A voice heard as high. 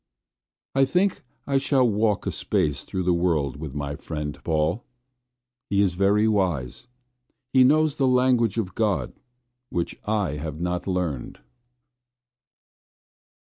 No: very low, 95 Hz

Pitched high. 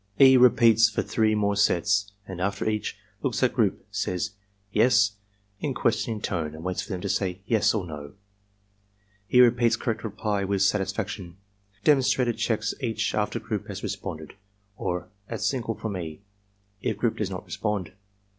No: low, 105 Hz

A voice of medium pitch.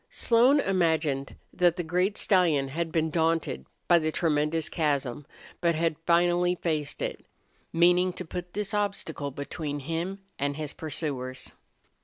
Yes: medium, 165 Hz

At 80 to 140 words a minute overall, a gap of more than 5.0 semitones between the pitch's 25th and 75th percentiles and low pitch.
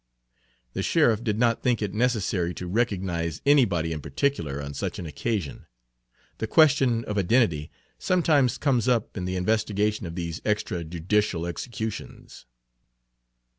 Yes: slow, 135 wpm; wide, 5.5 semitones; low, 105 Hz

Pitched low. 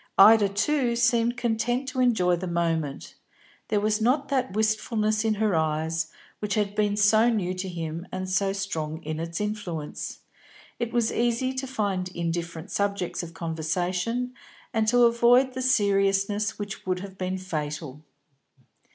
No: high, 200 Hz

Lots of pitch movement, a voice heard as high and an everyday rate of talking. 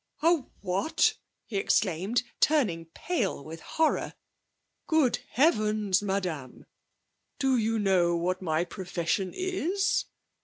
No: wide, 7.3 semitones; high, 200 Hz; slow, 105 wpm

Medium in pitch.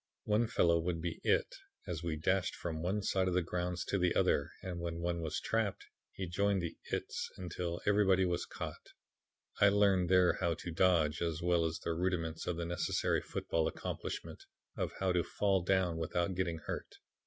No: very low, 90 Hz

